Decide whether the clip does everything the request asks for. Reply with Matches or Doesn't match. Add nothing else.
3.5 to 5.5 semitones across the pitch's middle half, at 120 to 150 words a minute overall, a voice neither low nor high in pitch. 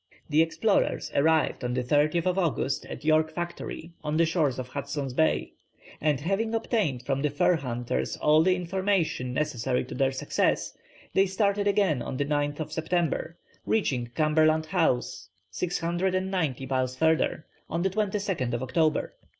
Matches